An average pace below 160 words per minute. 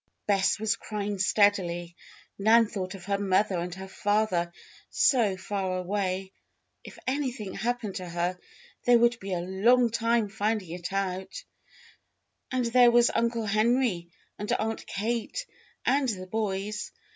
Yes: average, 140 wpm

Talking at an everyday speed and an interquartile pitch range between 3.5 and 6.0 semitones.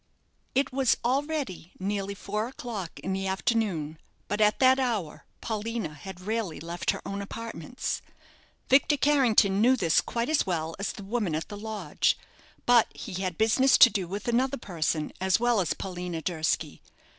Yes: average, 165 wpm; average, 5.0 semitones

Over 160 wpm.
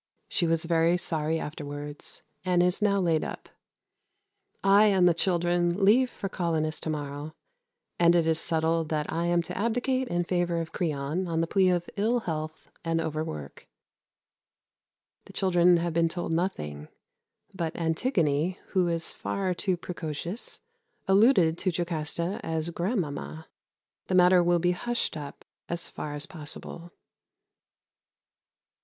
No: average, 145 wpm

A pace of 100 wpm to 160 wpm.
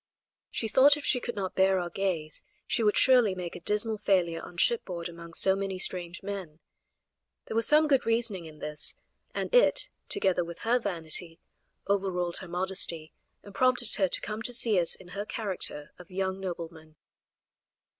No: average, 175 wpm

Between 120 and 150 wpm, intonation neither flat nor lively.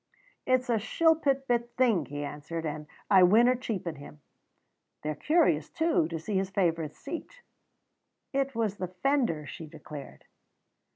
No: average, 140 wpm; wide, 8.7 semitones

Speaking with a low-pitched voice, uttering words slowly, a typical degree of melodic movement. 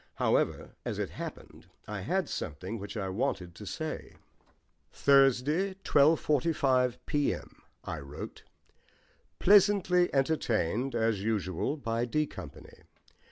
No: low, 130 Hz; slow, 110 wpm; wide, 7.0 semitones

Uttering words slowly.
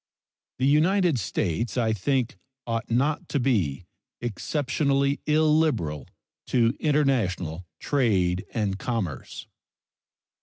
Yes: slow, 90 wpm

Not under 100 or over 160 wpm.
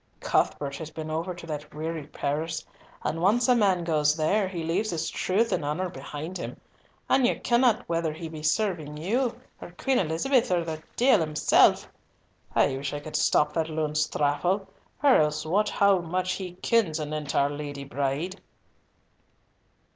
No: average, 170 wpm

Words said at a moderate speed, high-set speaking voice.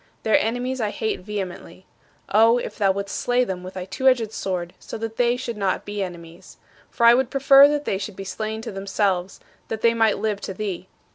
No: fast, 215 wpm; high, 210 Hz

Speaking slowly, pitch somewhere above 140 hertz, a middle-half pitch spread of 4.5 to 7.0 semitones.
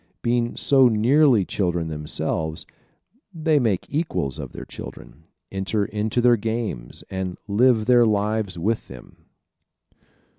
No: slow, 120 wpm; low, 110 Hz; average, 4.8 semitones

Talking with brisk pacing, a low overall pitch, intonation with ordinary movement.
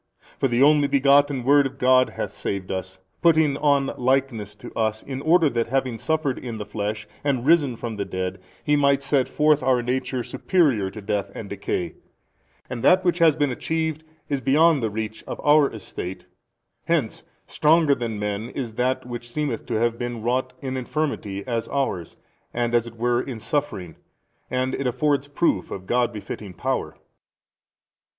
No: average, 175 wpm; low, 125 Hz; average, 4.4 semitones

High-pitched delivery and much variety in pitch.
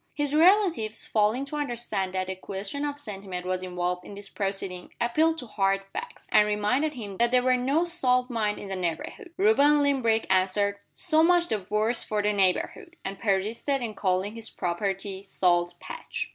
Yes: high, 215 Hz; wide, 6.4 semitones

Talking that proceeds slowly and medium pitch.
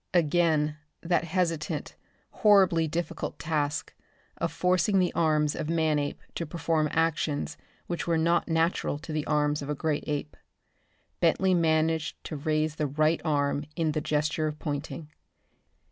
No: average, 145 wpm; medium, 155 Hz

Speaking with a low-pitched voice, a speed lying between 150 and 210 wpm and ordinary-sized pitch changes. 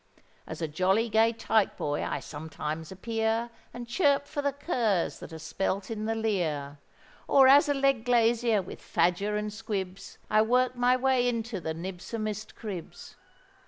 No: high, 220 Hz; average, 160 wpm; average, 4.7 semitones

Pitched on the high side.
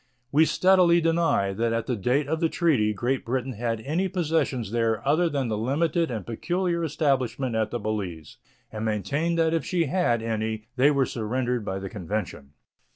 No: low, 125 Hz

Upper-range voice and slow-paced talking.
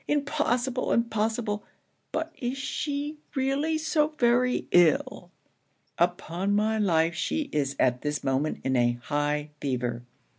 Yes: high, 210 Hz; slow, 120 wpm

